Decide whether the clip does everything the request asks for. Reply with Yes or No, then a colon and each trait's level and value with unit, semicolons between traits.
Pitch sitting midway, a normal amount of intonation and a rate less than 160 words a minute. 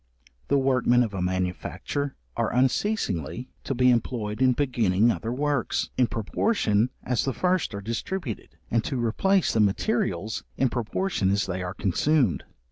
No: low, 120 Hz; average, 4.8 semitones; average, 150 wpm